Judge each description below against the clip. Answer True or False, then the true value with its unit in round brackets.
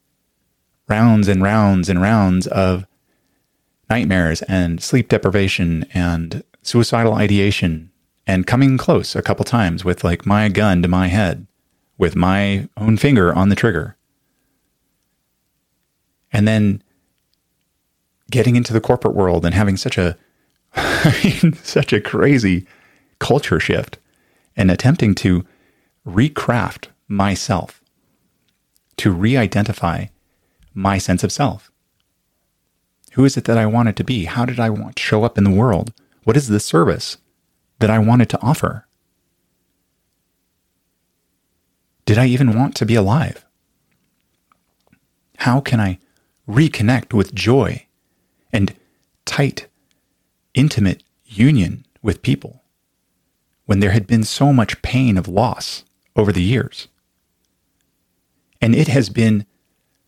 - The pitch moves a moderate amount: True (4.4 semitones)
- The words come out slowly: True (120 wpm)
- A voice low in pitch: True (100 Hz)